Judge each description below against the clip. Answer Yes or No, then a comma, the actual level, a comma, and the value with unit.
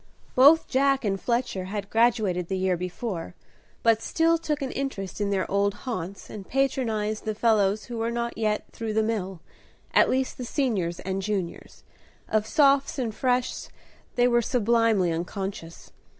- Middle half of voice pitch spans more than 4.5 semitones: No, average, 4.2 semitones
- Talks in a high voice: Yes, high, 220 Hz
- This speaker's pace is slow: No, average, 160 wpm